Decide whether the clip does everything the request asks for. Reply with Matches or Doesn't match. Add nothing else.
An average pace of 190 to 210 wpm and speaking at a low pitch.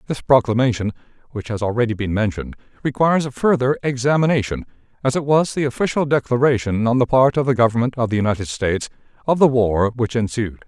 Doesn't match